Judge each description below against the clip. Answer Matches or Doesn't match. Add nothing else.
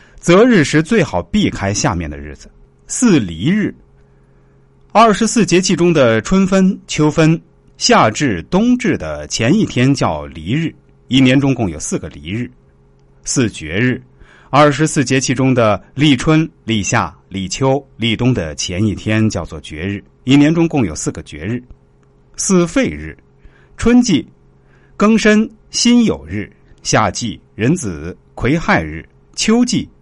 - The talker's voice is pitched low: Matches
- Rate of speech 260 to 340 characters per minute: Doesn't match